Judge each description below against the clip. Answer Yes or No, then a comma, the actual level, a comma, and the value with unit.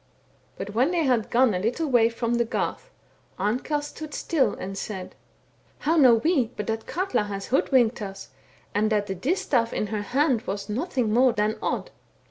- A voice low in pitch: No, high, 230 Hz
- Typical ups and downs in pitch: Yes, average, 4.4 semitones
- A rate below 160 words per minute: No, average, 185 wpm